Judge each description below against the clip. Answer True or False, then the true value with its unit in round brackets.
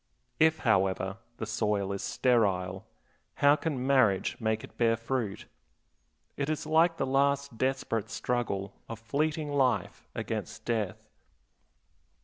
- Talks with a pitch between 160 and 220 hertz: False (120 Hz)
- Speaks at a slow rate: True (125 wpm)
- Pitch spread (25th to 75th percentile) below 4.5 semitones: False (5.1 semitones)